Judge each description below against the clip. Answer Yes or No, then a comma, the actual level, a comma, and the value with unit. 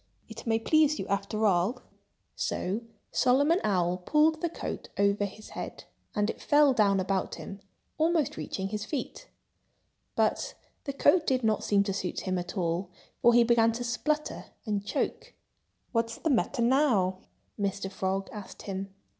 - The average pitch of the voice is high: Yes, high, 215 Hz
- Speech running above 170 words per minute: No, average, 160 wpm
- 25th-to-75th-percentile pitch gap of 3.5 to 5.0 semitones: No, wide, 5.6 semitones